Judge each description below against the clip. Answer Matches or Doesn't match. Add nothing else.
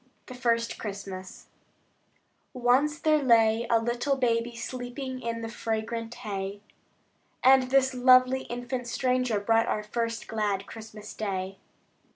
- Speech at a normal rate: Doesn't match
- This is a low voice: Doesn't match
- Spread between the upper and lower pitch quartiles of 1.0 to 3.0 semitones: Matches